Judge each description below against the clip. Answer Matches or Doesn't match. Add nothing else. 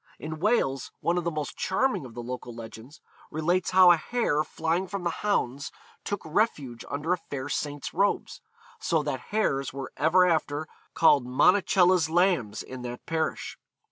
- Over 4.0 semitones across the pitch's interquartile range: Matches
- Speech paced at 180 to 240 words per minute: Doesn't match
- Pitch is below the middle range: Doesn't match